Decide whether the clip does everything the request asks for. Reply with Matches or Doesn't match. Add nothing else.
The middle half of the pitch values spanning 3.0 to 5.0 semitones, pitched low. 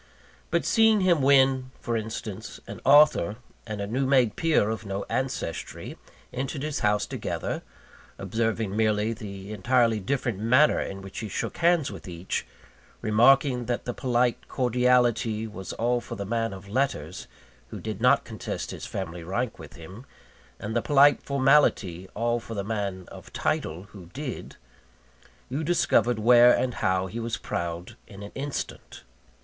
Matches